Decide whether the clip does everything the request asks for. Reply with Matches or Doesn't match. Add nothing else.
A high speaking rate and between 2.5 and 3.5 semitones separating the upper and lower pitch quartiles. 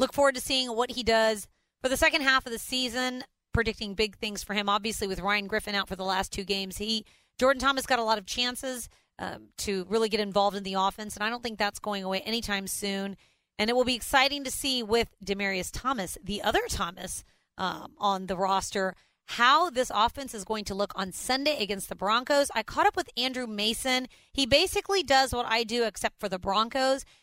Doesn't match